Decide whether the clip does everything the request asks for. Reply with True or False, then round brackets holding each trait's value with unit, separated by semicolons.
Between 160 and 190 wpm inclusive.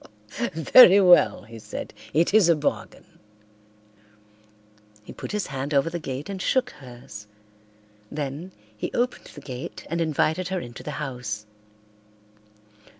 False (135 wpm)